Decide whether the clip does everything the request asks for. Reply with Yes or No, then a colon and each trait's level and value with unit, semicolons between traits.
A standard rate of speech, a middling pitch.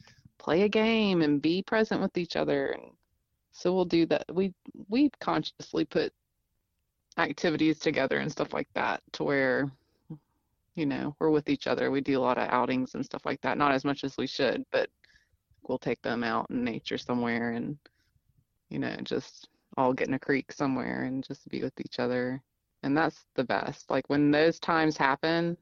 Yes: average, 190 wpm; medium, 145 Hz